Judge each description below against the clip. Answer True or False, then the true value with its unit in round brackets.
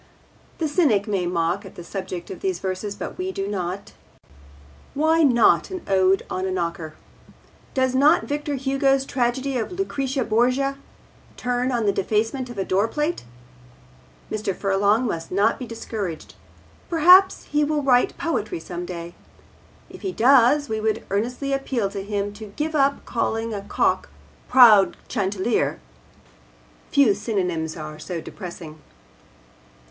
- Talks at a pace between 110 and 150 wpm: True (140 wpm)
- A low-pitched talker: False (220 Hz)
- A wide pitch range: True (6.1 semitones)